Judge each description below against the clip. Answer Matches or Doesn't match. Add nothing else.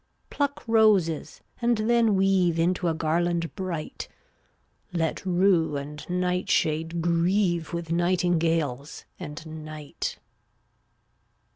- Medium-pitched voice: Matches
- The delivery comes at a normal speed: Doesn't match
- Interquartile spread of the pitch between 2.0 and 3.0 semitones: Matches